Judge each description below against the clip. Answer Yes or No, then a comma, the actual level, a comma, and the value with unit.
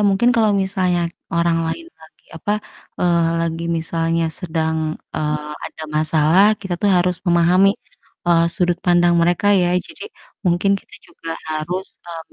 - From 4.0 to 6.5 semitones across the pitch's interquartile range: No, narrow, 2.5 semitones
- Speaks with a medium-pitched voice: Yes, medium, 175 Hz